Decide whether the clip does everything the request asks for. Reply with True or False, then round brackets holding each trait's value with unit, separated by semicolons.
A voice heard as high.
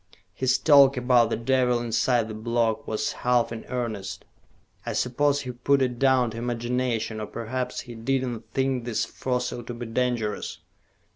False (120 Hz)